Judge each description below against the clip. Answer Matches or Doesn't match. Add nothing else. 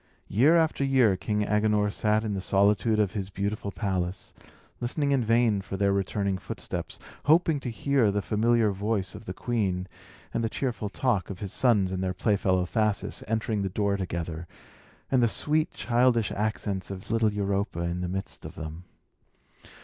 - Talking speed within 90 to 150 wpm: Doesn't match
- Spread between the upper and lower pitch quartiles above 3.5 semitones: Doesn't match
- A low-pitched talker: Matches